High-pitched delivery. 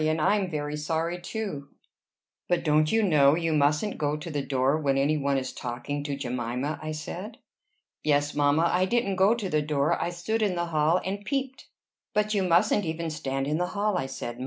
No: medium, 155 Hz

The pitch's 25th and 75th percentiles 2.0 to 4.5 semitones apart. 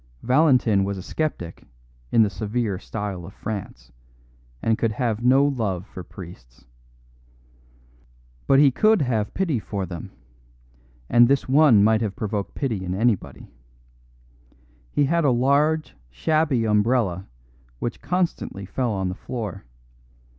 No: wide, 5.6 semitones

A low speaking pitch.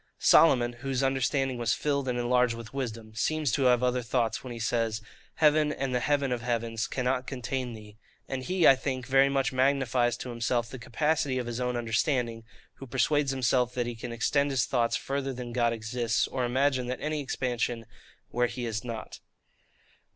Yes: low, 125 Hz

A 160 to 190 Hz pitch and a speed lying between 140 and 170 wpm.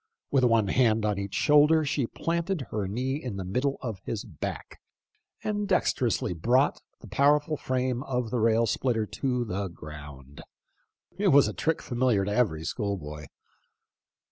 No: low, 120 Hz; average, 155 wpm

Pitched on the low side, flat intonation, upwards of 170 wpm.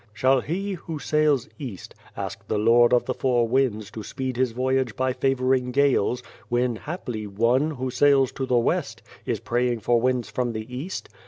Yes: low, 125 Hz; narrow, 2.0 semitones; average, 180 wpm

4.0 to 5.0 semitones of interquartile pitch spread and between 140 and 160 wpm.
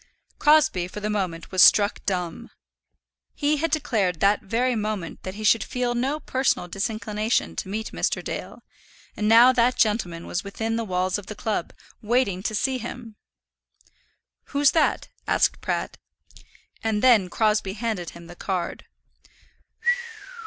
Yes: average, 4.3 semitones; average, 145 wpm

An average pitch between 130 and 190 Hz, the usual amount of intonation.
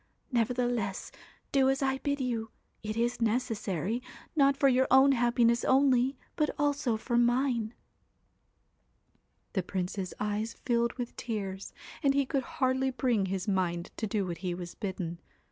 No: high, 240 Hz; average, 4.6 semitones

